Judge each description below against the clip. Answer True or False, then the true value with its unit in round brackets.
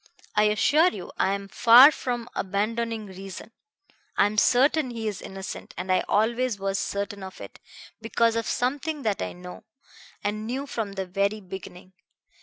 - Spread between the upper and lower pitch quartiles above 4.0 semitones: False (3.4 semitones)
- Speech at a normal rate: True (165 wpm)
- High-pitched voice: True (215 Hz)